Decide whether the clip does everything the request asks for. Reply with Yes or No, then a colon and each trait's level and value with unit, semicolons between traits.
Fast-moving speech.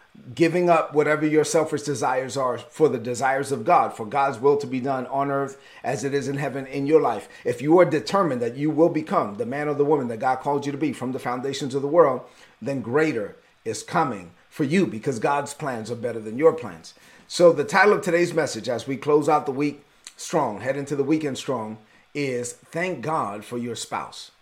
Yes: fast, 225 wpm